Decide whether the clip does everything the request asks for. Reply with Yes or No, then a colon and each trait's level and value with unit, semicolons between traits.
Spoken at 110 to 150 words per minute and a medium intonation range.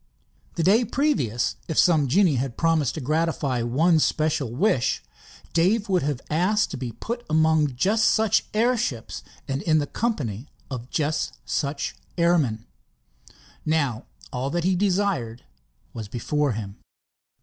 No: average, 140 wpm; wide, 6.3 semitones